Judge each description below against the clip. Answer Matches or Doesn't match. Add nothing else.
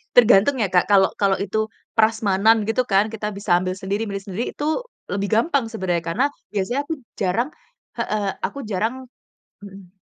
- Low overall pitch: Doesn't match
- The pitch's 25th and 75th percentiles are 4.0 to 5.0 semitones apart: Doesn't match